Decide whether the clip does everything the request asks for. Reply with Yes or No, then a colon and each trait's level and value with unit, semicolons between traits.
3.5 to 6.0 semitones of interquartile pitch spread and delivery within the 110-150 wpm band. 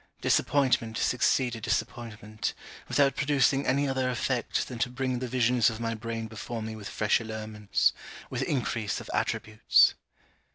No: average, 2.7 semitones; average, 140 wpm